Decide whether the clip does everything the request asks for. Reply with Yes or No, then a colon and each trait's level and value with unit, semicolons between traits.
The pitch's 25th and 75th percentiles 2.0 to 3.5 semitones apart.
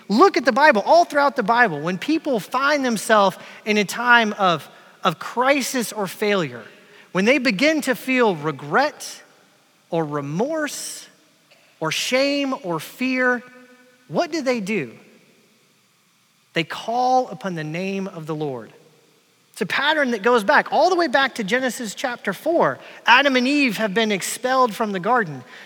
No: wide, 5.5 semitones